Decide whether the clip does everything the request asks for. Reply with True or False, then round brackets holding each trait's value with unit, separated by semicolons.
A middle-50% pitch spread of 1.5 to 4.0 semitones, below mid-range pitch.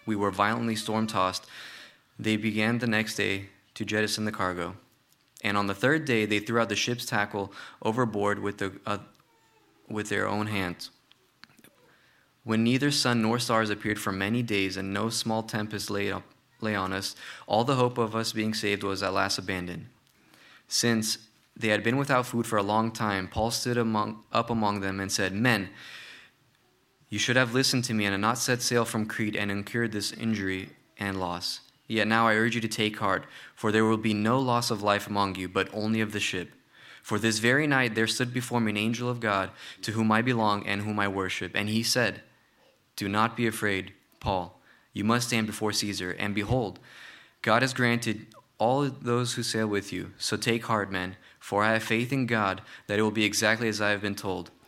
True (2.5 semitones; 110 Hz)